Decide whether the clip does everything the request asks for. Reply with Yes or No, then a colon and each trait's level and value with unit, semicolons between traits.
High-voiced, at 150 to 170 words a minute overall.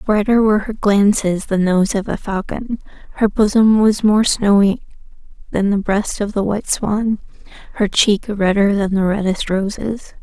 Yes: high, 205 Hz; average, 165 wpm